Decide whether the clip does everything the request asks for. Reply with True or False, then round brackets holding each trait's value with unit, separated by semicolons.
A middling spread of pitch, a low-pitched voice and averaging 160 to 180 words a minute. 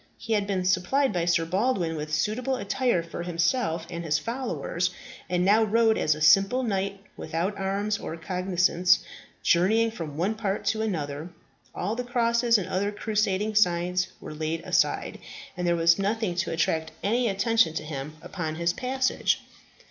False (4.7 semitones; 190 Hz; 165 wpm)